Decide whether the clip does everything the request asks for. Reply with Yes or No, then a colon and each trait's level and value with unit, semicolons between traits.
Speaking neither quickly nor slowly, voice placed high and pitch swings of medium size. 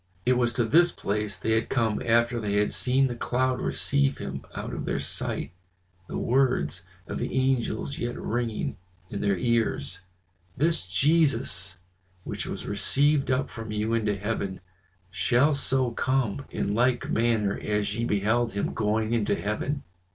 No: average, 160 wpm; low, 115 Hz; average, 3.9 semitones